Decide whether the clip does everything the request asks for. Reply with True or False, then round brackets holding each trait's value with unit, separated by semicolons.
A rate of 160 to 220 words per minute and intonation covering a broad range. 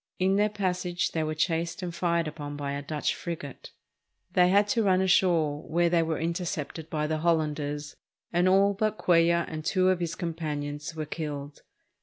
False (180 wpm; 3.0 semitones)